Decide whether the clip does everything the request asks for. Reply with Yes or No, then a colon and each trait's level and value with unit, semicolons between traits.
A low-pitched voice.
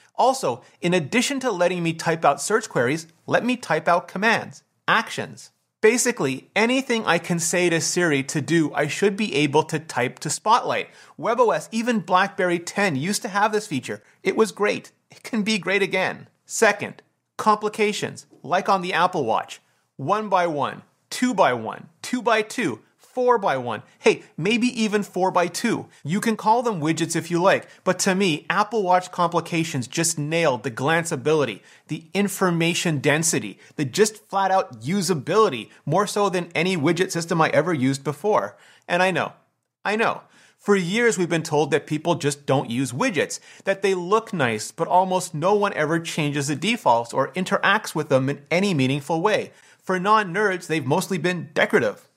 No: medium, 180 Hz